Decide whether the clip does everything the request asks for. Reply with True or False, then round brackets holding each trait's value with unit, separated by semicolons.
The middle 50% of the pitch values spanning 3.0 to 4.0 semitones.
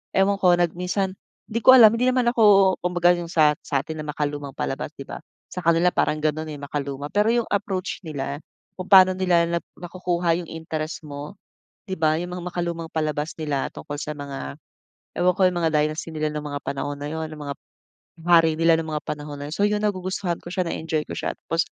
True (3.3 semitones)